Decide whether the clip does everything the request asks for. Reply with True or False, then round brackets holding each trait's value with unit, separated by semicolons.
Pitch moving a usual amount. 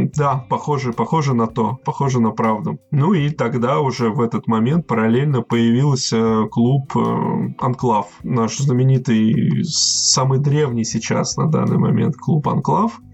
True (3.6 semitones)